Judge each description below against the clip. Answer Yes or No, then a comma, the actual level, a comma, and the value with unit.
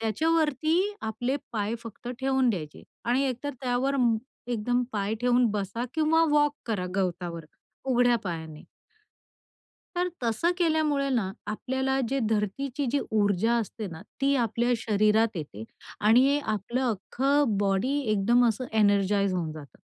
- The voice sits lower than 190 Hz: No, high, 230 Hz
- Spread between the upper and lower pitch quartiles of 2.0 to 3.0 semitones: No, average, 4.9 semitones